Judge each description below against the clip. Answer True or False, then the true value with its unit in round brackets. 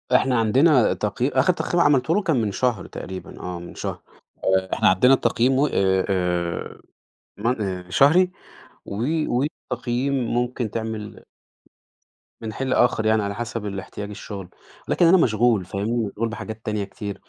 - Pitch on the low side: True (115 Hz)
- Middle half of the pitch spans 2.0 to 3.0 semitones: False (4.2 semitones)